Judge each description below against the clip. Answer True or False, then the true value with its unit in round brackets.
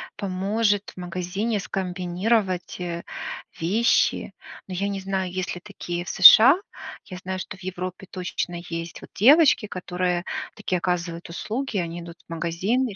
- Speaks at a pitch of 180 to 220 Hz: True (185 Hz)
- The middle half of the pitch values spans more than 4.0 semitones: False (2.4 semitones)